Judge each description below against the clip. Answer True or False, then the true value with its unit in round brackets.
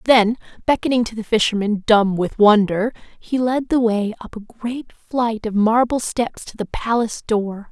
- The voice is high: True (225 Hz)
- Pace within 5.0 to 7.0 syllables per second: False (4.6 syllables/s)